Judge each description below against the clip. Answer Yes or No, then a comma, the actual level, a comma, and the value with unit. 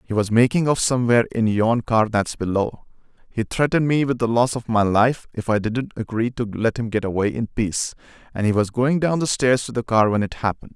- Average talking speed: No, fast, 235 wpm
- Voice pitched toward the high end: No, low, 115 Hz